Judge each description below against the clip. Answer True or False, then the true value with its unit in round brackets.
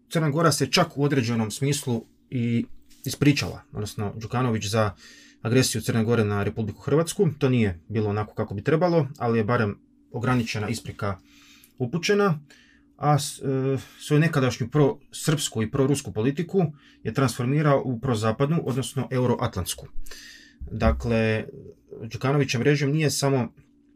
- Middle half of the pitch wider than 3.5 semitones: True (4.6 semitones)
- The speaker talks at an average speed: True (125 wpm)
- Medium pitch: False (130 Hz)